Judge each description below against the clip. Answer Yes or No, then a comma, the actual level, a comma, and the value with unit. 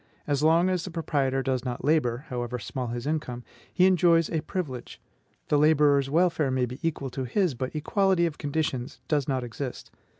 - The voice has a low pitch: No, medium, 145 Hz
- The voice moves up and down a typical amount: Yes, average, 4.2 semitones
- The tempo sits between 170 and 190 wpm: Yes, average, 180 wpm